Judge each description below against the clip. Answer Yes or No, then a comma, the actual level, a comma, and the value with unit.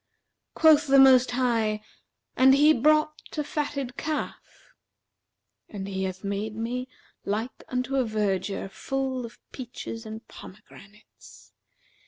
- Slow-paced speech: Yes, slow, 120 wpm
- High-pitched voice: Yes, high, 245 Hz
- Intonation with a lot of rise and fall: No, average, 4.2 semitones